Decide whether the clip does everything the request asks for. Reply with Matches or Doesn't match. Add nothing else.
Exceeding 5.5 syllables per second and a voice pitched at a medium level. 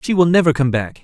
Matches